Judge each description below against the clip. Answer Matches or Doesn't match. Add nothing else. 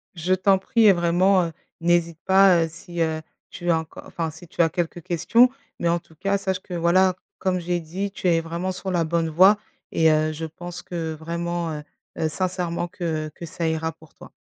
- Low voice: Doesn't match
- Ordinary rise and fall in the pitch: Doesn't match